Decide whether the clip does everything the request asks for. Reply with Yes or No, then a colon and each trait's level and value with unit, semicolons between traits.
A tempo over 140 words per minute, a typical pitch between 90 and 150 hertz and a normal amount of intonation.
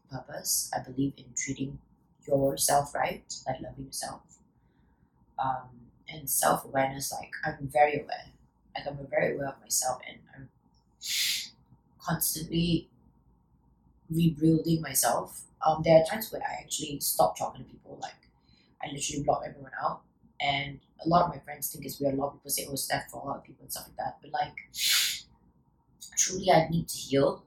Yes: average, 175 wpm; medium, 140 Hz; average, 3.0 semitones